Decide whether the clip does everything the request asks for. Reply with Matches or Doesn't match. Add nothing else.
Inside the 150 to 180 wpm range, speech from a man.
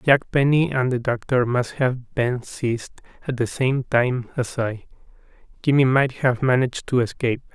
Matches